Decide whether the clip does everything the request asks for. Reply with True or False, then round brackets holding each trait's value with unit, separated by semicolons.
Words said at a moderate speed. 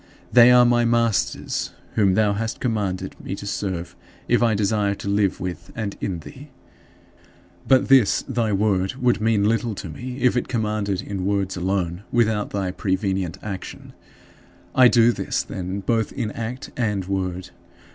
True (160 wpm)